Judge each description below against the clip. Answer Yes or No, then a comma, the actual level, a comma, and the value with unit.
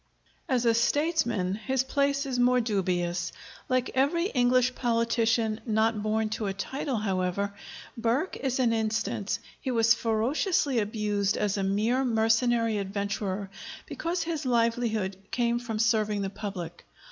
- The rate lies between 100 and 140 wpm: Yes, slow, 135 wpm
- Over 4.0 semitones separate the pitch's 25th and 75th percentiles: No, average, 3.4 semitones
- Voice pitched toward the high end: Yes, high, 225 Hz